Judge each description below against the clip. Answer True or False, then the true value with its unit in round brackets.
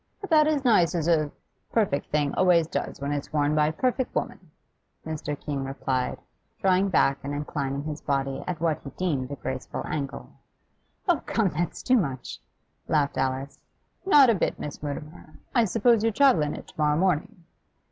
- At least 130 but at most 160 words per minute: False (175 wpm)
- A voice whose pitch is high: False (155 Hz)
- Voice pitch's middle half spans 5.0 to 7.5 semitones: True (5.6 semitones)